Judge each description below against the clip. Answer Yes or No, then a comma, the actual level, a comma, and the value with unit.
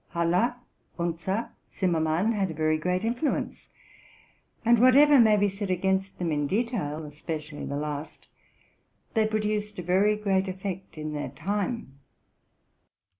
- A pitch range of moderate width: Yes, average, 4.9 semitones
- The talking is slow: Yes, slow, 130 wpm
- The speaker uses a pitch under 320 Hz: Yes, high, 190 Hz